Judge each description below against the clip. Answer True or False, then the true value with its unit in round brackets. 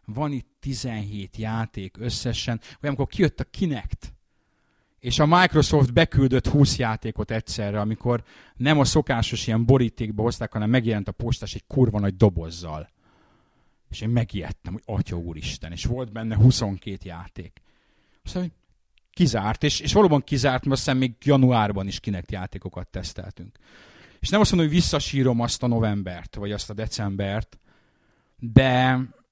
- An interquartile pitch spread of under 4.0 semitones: False (4.6 semitones)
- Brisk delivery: False (145 wpm)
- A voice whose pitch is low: True (115 Hz)